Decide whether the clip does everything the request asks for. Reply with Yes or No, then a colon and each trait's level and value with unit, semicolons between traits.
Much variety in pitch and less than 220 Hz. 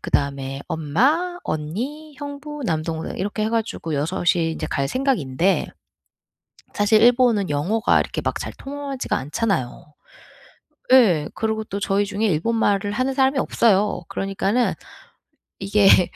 Yes: wide, 7.5 semitones; high, 205 Hz